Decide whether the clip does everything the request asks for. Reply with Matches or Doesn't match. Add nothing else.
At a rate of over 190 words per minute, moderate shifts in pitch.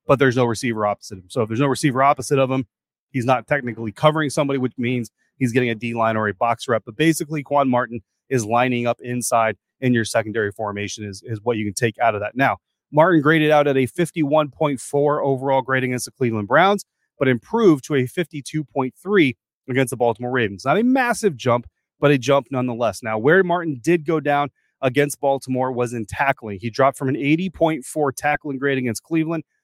Matches